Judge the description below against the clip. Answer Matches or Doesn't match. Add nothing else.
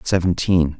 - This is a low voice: Matches